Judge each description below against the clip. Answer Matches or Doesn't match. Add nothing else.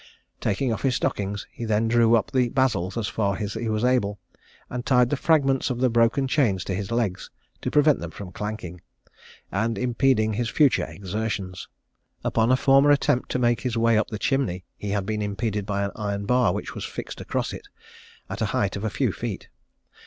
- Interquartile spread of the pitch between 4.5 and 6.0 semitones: Doesn't match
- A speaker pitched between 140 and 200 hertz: Doesn't match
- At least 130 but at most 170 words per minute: Doesn't match